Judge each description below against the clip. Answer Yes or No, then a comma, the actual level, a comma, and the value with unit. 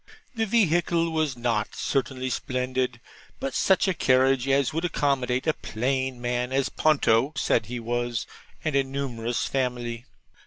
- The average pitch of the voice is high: No, low, 130 Hz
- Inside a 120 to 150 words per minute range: Yes, average, 145 wpm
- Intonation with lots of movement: No, average, 2.8 semitones